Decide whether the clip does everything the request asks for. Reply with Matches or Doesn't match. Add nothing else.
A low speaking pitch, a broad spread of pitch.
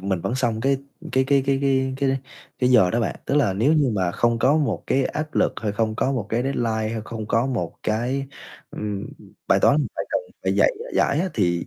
Doesn't match